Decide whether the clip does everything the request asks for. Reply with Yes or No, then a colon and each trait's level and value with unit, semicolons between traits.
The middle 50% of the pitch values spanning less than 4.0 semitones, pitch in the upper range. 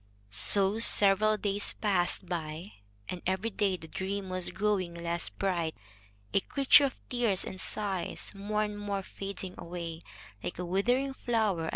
Yes: average, 3.0 semitones; high, 195 Hz